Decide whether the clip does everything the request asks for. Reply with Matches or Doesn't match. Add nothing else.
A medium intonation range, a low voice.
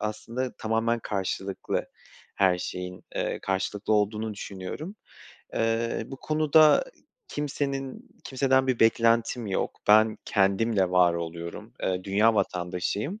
Matches